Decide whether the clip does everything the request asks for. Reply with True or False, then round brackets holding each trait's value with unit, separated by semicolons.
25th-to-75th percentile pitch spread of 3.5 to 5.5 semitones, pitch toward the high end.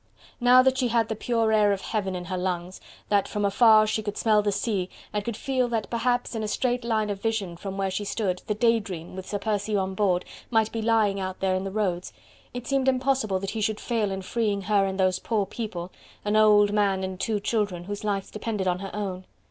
False (2.7 semitones; 210 Hz)